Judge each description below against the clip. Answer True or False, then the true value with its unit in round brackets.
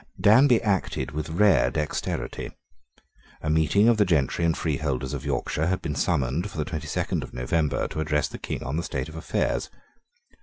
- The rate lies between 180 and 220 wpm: True (185 wpm)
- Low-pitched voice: True (80 Hz)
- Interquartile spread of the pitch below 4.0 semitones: True (3.6 semitones)